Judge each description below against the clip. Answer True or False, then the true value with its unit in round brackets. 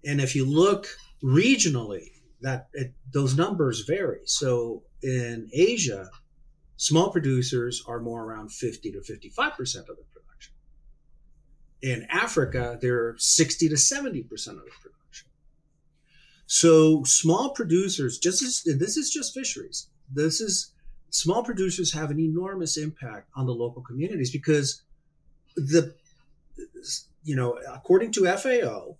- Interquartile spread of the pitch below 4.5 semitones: False (5.3 semitones)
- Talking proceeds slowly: True (125 wpm)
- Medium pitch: True (150 Hz)